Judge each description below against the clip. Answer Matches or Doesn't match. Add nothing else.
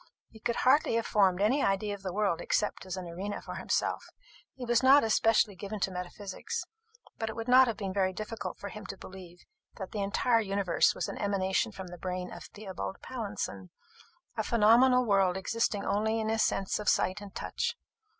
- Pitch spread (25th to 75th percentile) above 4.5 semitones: Doesn't match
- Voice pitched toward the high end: Matches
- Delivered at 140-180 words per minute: Doesn't match